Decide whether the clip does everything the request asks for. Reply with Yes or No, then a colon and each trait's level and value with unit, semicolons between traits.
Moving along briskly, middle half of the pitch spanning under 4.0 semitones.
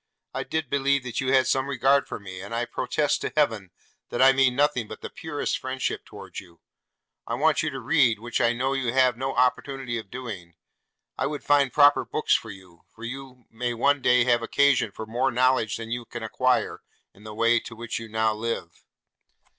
Yes: fast, 210 wpm; average, 3.0 semitones